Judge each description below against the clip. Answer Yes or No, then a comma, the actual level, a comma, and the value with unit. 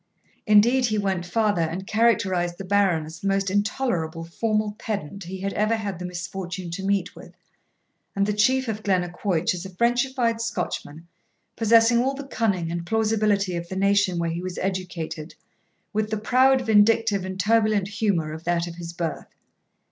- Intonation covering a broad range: No, average, 3.9 semitones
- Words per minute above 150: Yes, average, 170 wpm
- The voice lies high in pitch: Yes, high, 200 Hz